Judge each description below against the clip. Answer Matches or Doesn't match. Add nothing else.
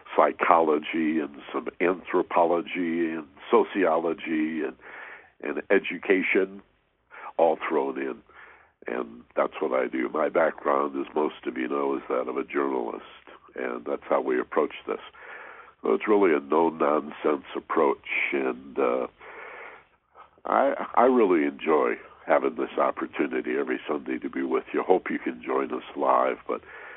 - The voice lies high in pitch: Matches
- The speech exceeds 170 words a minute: Doesn't match